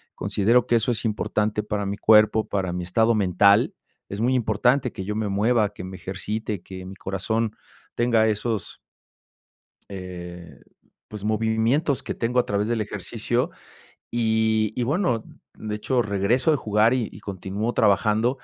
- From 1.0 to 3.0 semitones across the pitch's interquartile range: Yes, narrow, 2.6 semitones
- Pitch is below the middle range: Yes, low, 110 Hz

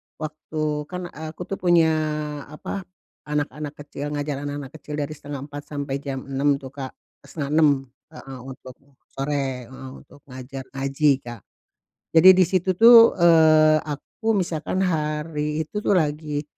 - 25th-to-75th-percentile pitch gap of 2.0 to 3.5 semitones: Yes, narrow, 2.5 semitones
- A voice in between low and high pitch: Yes, medium, 150 Hz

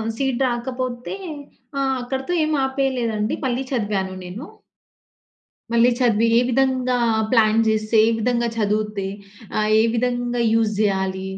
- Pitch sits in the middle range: No, high, 235 Hz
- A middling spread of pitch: Yes, average, 3.0 semitones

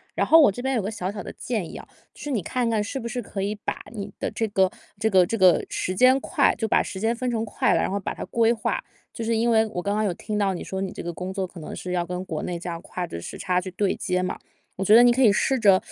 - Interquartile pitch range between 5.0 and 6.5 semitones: No, average, 3.7 semitones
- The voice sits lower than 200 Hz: No, high, 205 Hz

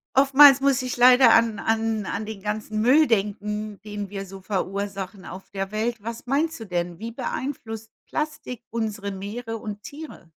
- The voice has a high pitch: Yes, high, 220 Hz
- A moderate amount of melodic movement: Yes, average, 3.4 semitones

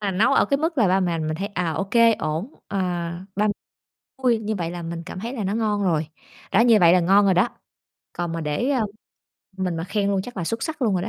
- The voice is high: Yes, high, 195 Hz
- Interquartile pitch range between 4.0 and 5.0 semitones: Yes, average, 4.5 semitones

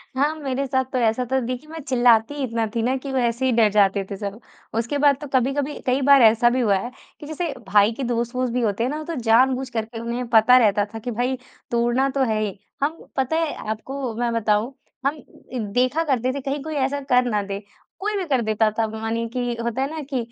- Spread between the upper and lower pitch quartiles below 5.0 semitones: Yes, average, 3.3 semitones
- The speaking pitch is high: Yes, very high, 250 Hz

